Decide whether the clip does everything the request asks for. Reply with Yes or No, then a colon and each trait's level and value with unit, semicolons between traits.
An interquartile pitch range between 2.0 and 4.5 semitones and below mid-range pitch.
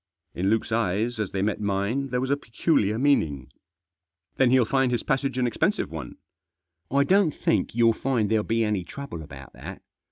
No: wide, 5.4 semitones; low, 115 Hz